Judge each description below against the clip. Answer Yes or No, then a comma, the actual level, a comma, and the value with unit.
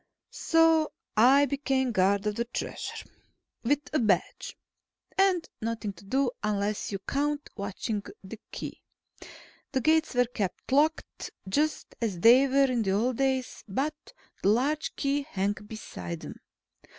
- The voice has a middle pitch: No, high, 245 Hz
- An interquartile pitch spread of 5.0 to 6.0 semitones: Yes, wide, 5.6 semitones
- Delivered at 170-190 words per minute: No, average, 140 wpm